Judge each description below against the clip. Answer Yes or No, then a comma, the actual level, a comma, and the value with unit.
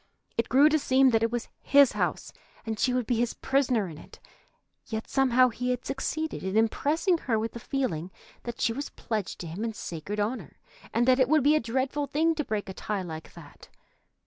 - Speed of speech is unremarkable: No, fast, 215 wpm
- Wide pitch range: No, average, 3.8 semitones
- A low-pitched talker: No, high, 240 Hz